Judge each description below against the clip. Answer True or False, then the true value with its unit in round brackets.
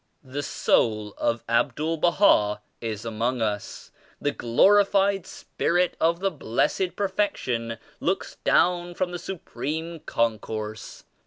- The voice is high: False (145 Hz)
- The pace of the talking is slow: True (115 wpm)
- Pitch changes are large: True (7.7 semitones)